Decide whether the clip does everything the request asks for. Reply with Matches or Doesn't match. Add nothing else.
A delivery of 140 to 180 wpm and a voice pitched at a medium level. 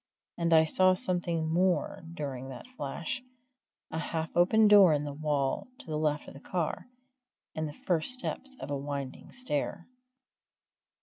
Matches